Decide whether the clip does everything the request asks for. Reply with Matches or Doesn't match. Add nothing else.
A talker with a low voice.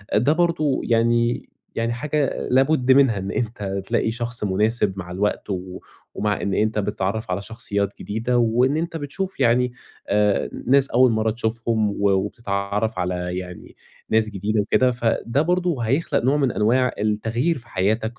Matches